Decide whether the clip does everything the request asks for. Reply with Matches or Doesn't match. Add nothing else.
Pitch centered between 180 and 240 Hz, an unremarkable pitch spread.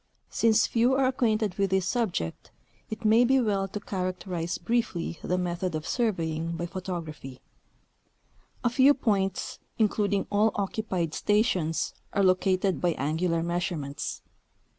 Matches